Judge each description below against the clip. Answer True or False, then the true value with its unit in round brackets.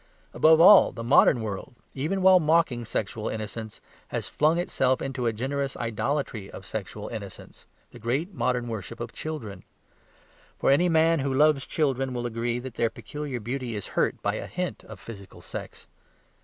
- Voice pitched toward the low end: True (125 Hz)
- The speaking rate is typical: True (170 wpm)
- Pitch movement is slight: False (4.9 semitones)